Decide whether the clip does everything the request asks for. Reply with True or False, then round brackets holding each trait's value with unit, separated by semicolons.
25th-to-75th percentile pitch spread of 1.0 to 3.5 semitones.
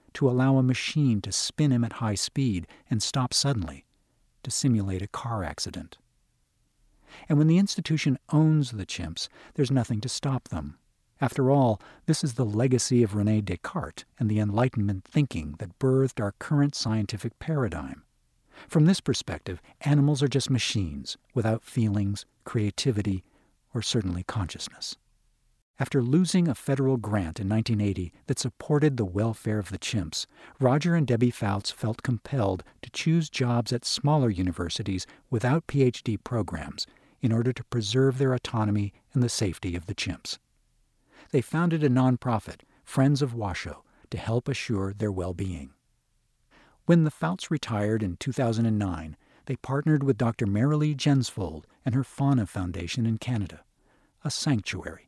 False (5.2 semitones)